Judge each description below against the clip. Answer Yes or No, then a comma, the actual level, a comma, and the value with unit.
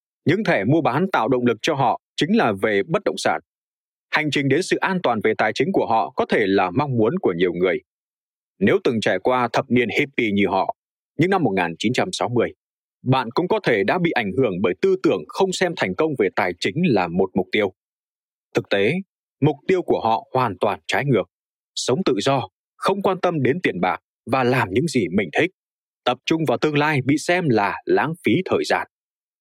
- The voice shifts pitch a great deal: Yes, wide, 6.7 semitones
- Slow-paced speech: No, average, 215 wpm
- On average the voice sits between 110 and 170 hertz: Yes, medium, 140 Hz